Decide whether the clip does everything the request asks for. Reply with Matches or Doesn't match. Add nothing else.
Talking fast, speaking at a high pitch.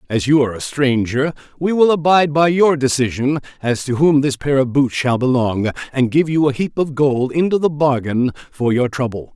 Doesn't match